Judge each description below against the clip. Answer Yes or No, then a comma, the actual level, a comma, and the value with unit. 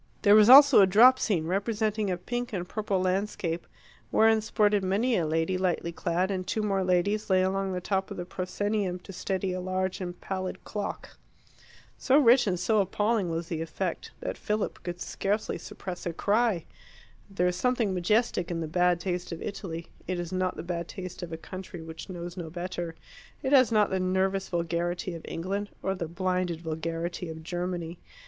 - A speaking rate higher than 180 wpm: Yes, average, 190 wpm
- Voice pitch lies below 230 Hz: Yes, medium, 185 Hz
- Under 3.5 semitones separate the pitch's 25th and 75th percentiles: Yes, average, 2.8 semitones